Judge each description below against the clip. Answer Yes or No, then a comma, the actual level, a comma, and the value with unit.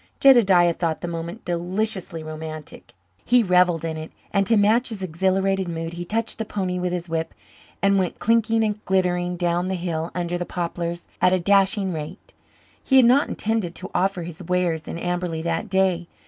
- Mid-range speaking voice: Yes, medium, 180 Hz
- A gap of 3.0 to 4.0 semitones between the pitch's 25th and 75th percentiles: No, narrow, 2.6 semitones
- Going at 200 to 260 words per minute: No, average, 185 wpm